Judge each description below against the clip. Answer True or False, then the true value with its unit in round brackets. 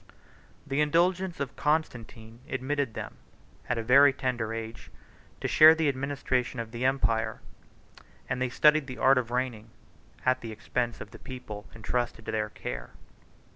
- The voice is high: False (125 Hz)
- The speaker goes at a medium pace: True (155 wpm)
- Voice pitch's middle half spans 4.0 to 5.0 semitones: False (3.5 semitones)